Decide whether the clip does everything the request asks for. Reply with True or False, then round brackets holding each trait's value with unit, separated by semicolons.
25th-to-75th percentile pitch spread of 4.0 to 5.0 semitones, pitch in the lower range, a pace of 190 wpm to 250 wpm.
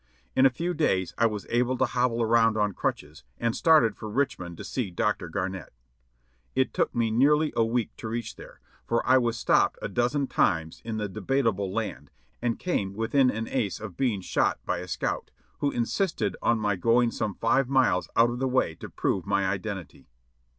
True (4.3 semitones; 115 Hz; 195 wpm)